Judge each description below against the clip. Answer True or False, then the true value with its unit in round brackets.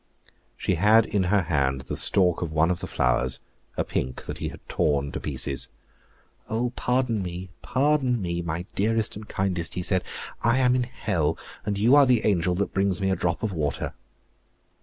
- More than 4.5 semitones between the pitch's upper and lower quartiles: True (5.1 semitones)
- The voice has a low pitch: True (95 Hz)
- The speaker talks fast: False (190 wpm)